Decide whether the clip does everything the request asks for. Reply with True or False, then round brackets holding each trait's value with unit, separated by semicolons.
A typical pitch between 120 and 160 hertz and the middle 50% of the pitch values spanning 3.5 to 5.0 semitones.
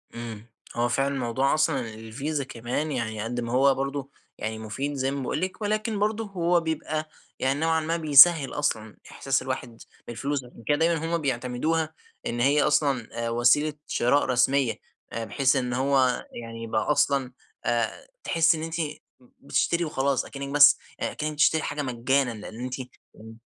True (135 Hz; 4.2 semitones)